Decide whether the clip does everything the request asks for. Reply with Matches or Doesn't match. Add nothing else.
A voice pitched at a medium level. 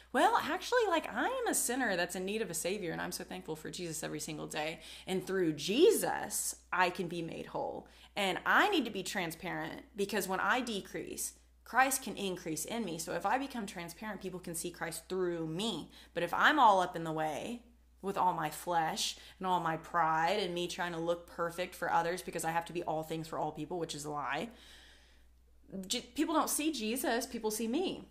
Matches